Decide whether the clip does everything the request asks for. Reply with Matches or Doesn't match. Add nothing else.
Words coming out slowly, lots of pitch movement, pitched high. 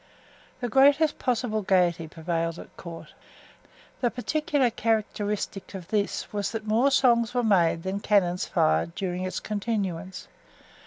Doesn't match